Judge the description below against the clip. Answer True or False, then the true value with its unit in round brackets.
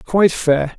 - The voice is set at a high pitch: False (170 Hz)